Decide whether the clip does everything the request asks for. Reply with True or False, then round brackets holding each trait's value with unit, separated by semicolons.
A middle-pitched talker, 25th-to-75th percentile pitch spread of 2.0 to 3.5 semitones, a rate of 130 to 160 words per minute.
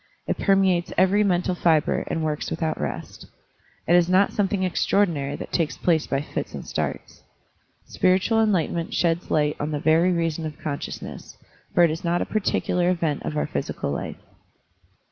False (170 Hz; 2.9 semitones; 170 wpm)